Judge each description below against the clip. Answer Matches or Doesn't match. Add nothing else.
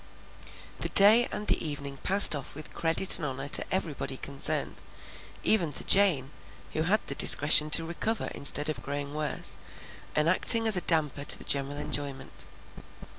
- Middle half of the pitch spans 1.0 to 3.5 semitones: Doesn't match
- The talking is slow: Doesn't match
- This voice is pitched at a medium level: Matches